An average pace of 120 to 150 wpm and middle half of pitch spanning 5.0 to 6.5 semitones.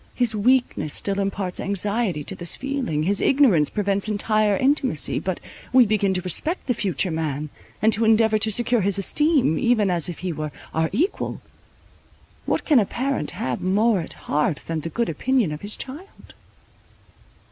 No: average, 170 wpm; wide, 5.6 semitones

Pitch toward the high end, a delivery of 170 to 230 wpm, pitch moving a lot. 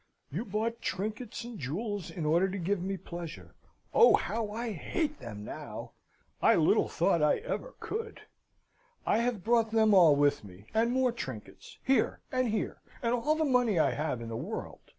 Yes: high, 210 Hz; average, 180 wpm; wide, 6.4 semitones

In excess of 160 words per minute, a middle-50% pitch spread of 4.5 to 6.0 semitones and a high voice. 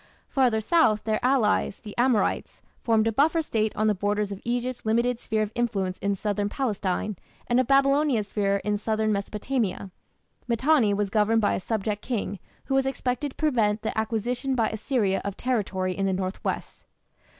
No: average, 175 wpm; average, 3.4 semitones; high, 220 Hz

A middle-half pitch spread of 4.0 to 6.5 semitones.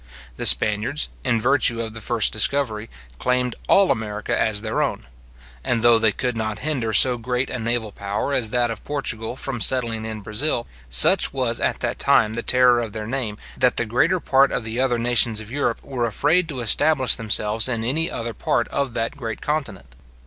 No: average, 2.9 semitones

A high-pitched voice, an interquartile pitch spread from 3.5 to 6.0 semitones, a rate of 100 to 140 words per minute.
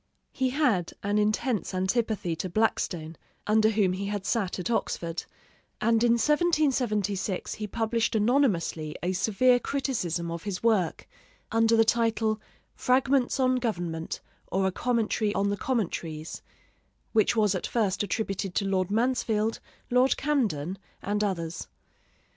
Yes: high, 215 Hz; average, 4.2 semitones; slow, 135 wpm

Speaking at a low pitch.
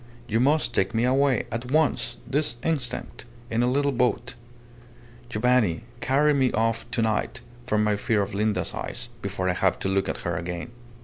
Yes: low, 120 Hz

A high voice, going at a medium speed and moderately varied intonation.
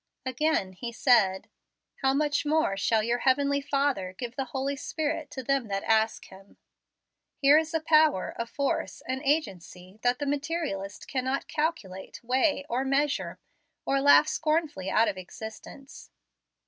Yes: very high, 265 Hz; average, 150 wpm; average, 5.0 semitones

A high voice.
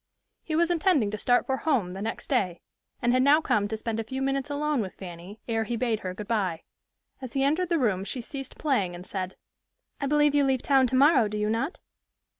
Yes: high, 245 Hz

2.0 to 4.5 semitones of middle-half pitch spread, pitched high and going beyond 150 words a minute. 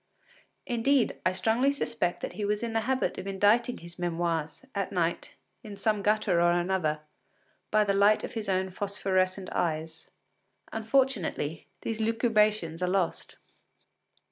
No: average, 4.0 semitones; high, 200 Hz; average, 145 wpm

